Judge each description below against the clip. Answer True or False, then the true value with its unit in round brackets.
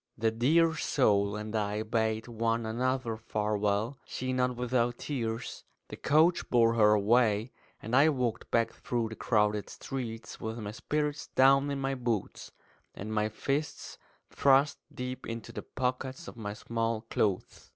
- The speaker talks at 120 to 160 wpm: True (150 wpm)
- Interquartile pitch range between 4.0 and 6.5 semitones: False (3.1 semitones)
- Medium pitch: False (115 Hz)